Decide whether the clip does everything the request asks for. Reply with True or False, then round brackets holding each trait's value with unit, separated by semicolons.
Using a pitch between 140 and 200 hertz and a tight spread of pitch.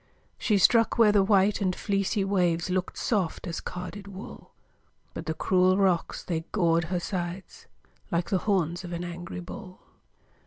True (185 Hz; 2.3 semitones)